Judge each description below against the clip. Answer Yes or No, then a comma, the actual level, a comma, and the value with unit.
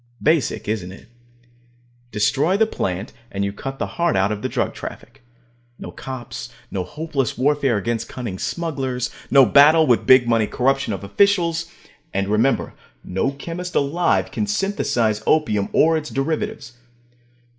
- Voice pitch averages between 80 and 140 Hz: Yes, low, 135 Hz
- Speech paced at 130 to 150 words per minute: Yes, average, 145 wpm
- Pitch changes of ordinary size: No, wide, 7.0 semitones